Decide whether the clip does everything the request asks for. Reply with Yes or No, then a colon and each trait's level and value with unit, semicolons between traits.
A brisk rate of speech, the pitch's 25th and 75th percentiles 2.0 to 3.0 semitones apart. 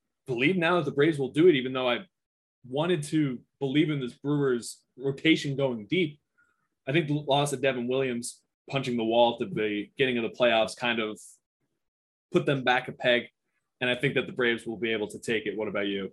No: fast, 215 wpm; average, 3.8 semitones